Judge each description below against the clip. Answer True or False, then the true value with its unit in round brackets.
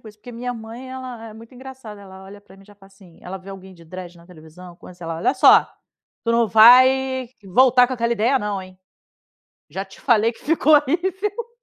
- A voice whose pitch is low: False (220 Hz)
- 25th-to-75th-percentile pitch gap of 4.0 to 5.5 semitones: True (5.2 semitones)